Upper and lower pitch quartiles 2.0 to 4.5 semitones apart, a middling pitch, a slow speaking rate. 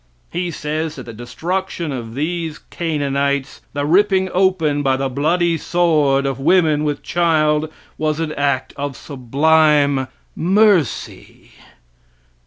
Yes: average, 3.4 semitones; medium, 150 Hz; slow, 120 wpm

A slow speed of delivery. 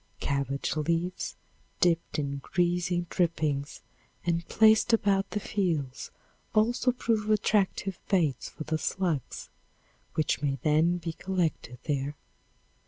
Yes: slow, 110 wpm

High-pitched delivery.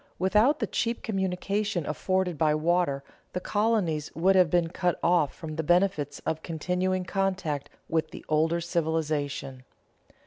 No: medium, 175 Hz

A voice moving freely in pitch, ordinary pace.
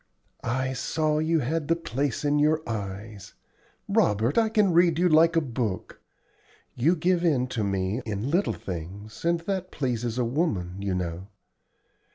Yes: wide, 7.8 semitones; average, 165 wpm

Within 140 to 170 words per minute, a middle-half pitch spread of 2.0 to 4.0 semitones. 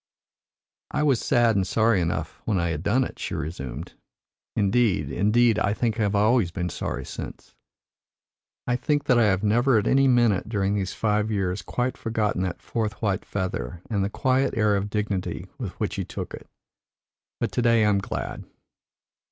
No: average, 185 wpm; average, 3.7 semitones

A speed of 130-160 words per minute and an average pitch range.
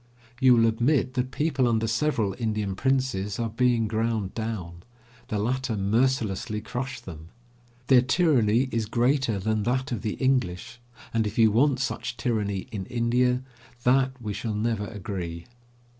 Yes: average, 150 wpm; average, 3.4 semitones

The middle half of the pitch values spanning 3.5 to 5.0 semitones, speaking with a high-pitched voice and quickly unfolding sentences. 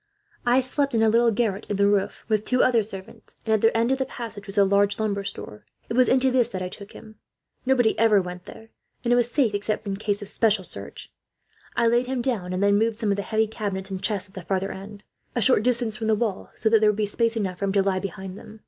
No: average, 2.7 semitones; high, 215 Hz; fast, 270 wpm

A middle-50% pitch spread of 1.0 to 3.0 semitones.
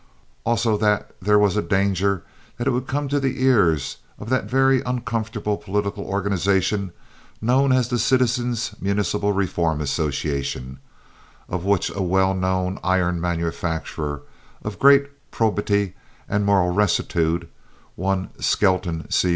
No: average, 4.3 semitones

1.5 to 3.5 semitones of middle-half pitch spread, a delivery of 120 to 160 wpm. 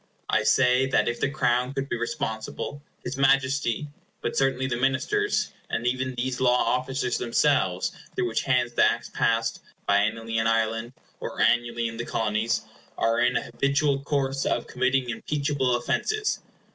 Yes: narrow, 2.6 semitones; average, 145 wpm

